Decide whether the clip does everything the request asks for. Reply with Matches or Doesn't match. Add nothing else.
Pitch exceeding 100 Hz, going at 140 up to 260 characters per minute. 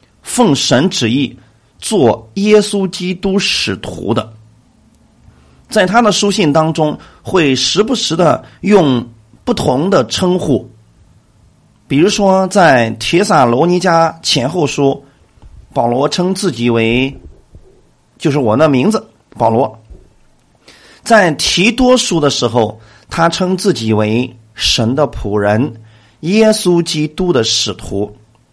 Matches